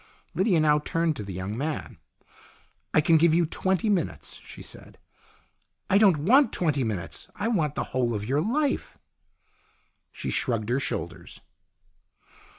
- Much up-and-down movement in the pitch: Yes, wide, 6.8 semitones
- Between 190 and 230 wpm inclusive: No, average, 155 wpm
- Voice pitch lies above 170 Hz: No, medium, 155 Hz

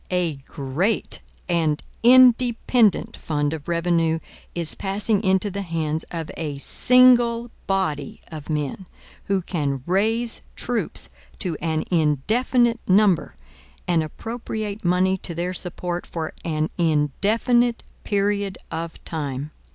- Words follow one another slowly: Yes, slow, 115 wpm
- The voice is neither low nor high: Yes, medium, 180 Hz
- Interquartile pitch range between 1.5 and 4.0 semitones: No, average, 5.3 semitones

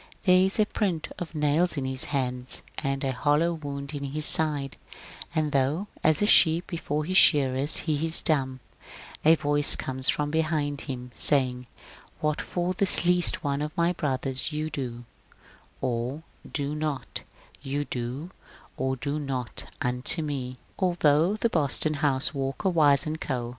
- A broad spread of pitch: No, average, 3.2 semitones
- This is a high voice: No, medium, 145 Hz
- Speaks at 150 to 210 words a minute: Yes, average, 160 wpm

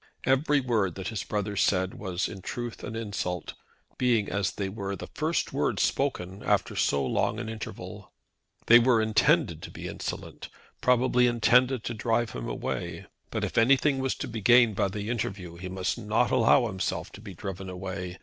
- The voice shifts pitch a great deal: No, average, 4.0 semitones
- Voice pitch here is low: Yes, low, 110 Hz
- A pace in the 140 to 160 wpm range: No, average, 180 wpm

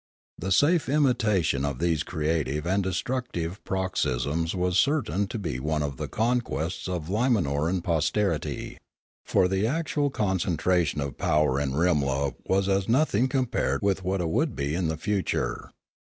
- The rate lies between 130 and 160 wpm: Yes, average, 150 wpm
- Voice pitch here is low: Yes, very low, 90 Hz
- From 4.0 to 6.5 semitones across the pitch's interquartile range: Yes, wide, 5.5 semitones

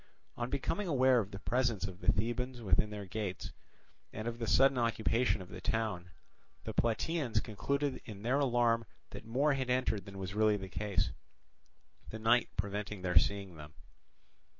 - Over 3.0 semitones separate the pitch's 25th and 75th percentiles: Yes, average, 3.9 semitones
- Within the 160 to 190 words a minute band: Yes, average, 170 wpm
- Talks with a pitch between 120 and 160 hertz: No, low, 110 Hz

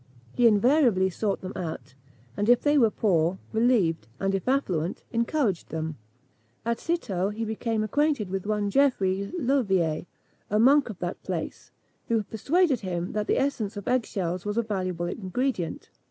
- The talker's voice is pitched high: Yes, high, 210 Hz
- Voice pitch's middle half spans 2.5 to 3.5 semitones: No, average, 4.8 semitones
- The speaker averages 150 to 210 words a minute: Yes, average, 160 wpm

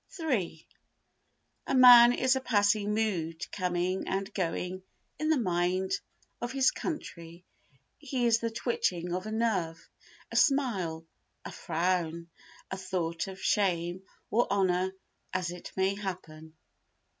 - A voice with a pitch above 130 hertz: Yes, high, 190 Hz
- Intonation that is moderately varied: Yes, average, 4.8 semitones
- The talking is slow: Yes, slow, 130 wpm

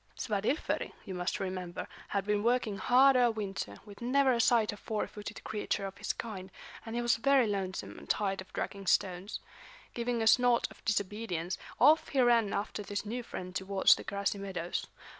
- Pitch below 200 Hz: No, high, 210 Hz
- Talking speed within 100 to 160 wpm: No, average, 185 wpm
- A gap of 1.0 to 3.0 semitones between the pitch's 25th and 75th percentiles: No, average, 3.5 semitones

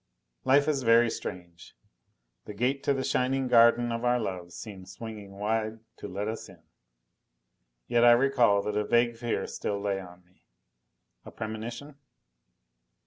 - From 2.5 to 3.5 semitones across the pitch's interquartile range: Yes, average, 3.2 semitones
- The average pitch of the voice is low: Yes, low, 115 Hz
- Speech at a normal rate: Yes, average, 150 wpm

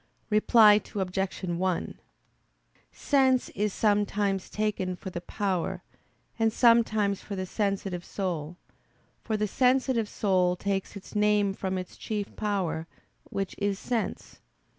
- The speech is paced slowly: Yes, slow, 120 wpm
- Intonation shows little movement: Yes, narrow, 2.2 semitones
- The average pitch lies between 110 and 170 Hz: No, high, 200 Hz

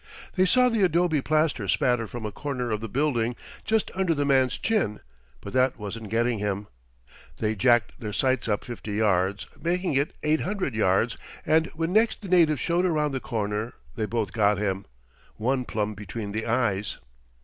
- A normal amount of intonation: No, wide, 6.5 semitones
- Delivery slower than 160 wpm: No, average, 175 wpm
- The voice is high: No, low, 120 Hz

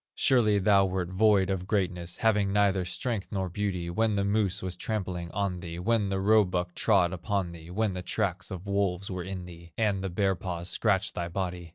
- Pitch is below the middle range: Yes, very low, 95 Hz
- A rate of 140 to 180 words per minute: No, average, 200 wpm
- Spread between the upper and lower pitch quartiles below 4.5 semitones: Yes, narrow, 2.4 semitones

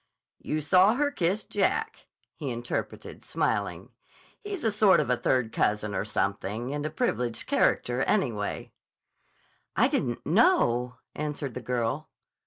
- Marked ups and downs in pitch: Yes, wide, 8.5 semitones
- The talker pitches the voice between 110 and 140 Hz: Yes, low, 135 Hz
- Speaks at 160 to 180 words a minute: No, slow, 135 wpm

